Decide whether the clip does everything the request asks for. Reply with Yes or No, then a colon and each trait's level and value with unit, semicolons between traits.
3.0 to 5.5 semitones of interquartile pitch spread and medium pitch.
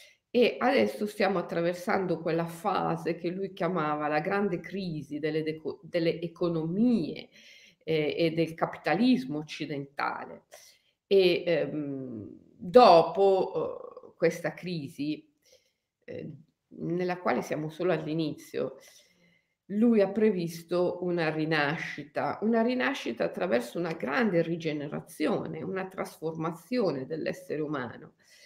Yes: average, 4.1 semitones; medium, 175 Hz